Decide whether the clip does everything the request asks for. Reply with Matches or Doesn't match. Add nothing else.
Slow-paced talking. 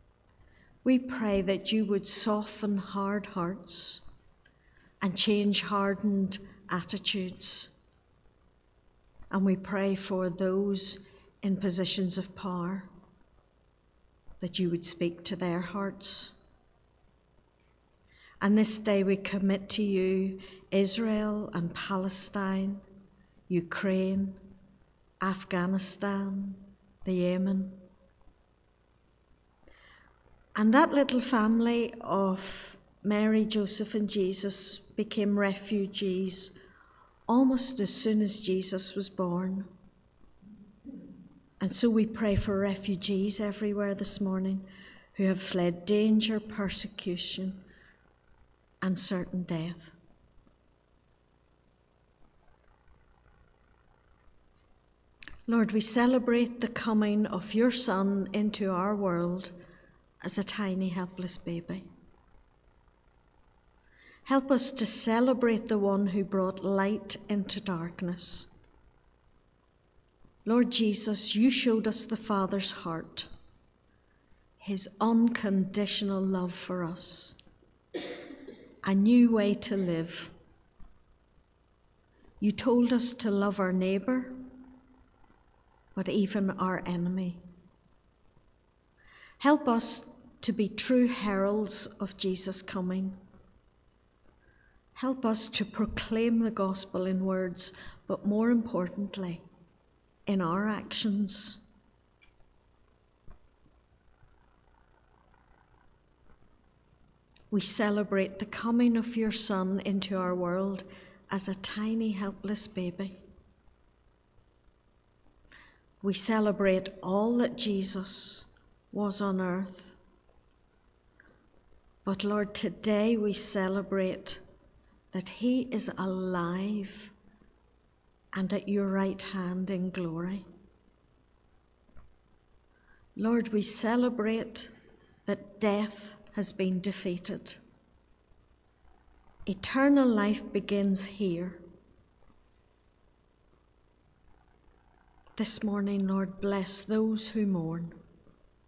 Matches